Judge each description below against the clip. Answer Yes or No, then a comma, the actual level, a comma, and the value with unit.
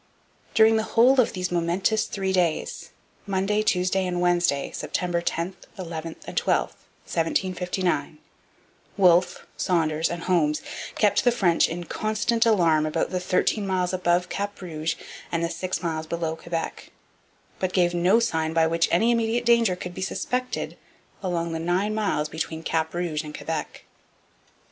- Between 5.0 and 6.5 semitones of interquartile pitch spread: No, average, 2.9 semitones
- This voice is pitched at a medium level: Yes, medium, 180 Hz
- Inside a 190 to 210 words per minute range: No, average, 150 wpm